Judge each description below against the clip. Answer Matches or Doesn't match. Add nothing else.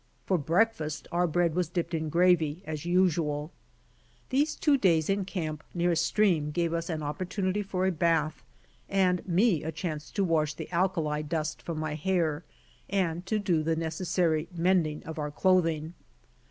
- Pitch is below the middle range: Doesn't match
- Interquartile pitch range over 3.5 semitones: Doesn't match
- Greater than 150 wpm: Matches